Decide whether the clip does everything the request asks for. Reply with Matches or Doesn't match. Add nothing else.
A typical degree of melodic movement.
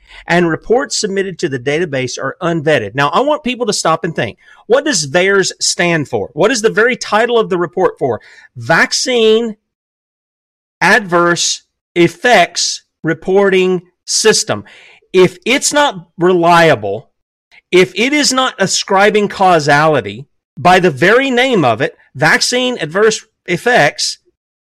Doesn't match